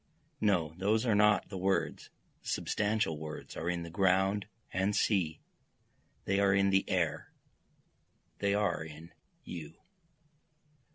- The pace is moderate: No, slow, 130 wpm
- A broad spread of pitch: No, average, 3.4 semitones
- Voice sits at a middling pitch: No, very low, 95 Hz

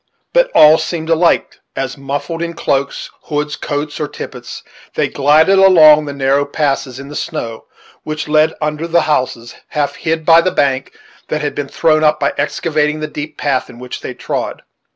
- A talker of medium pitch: Yes, medium, 150 Hz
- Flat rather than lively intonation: Yes, narrow, 2.1 semitones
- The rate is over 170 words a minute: Yes, average, 180 wpm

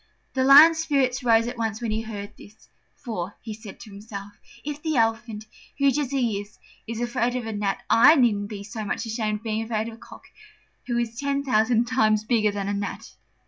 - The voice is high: Yes, high, 225 Hz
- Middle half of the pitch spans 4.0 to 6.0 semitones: No, average, 2.7 semitones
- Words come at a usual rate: No, fast, 215 wpm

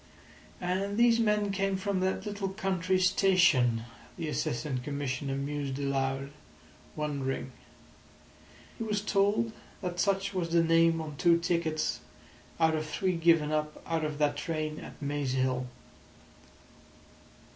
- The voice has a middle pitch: Yes, medium, 165 Hz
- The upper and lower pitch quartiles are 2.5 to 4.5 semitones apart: No, average, 4.9 semitones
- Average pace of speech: No, slow, 130 wpm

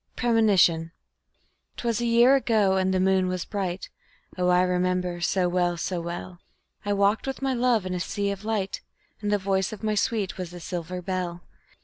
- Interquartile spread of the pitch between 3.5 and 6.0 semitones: No, average, 2.9 semitones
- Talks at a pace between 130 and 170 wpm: No, average, 190 wpm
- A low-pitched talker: No, high, 190 Hz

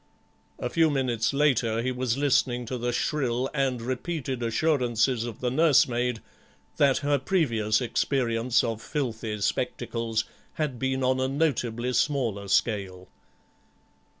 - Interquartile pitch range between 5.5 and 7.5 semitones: No, average, 3.0 semitones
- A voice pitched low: Yes, low, 125 Hz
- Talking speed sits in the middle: No, slow, 125 wpm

